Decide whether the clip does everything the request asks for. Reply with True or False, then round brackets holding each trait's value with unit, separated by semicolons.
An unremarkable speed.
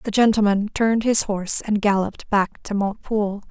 True (170 wpm)